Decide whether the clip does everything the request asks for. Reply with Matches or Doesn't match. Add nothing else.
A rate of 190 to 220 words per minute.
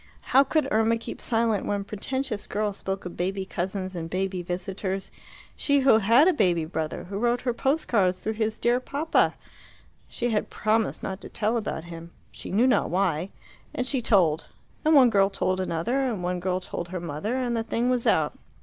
Matches